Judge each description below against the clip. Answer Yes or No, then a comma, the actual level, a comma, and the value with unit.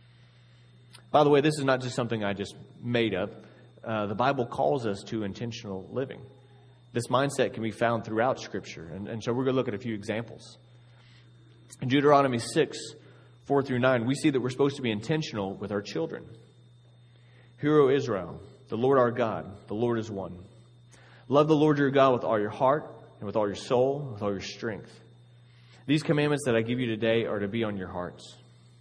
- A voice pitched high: No, low, 120 Hz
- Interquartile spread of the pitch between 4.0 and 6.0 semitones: No, narrow, 2.4 semitones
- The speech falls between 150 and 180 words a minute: No, average, 200 wpm